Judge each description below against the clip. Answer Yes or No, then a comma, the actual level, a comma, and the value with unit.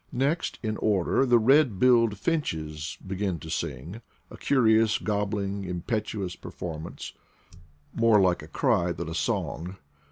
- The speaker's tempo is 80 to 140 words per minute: Yes, slow, 135 wpm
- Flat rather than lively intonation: No, average, 4.5 semitones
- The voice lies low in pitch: Yes, low, 100 Hz